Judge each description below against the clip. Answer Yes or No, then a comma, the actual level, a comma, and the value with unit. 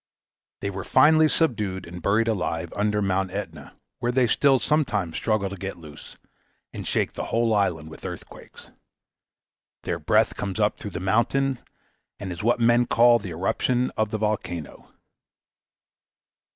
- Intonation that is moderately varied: Yes, average, 4.0 semitones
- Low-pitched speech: Yes, low, 105 Hz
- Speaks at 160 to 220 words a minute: No, average, 150 wpm